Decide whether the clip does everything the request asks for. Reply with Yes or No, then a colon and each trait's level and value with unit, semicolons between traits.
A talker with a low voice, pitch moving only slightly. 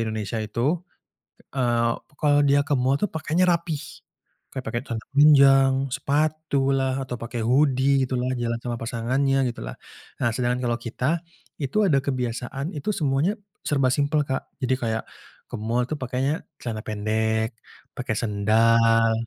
No: low, 125 Hz; average, 3.3 semitones